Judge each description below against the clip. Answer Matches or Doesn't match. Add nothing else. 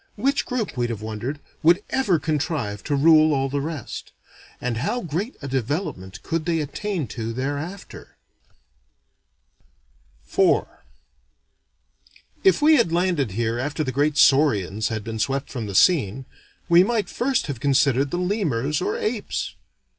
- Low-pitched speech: Doesn't match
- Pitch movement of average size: Doesn't match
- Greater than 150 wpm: Doesn't match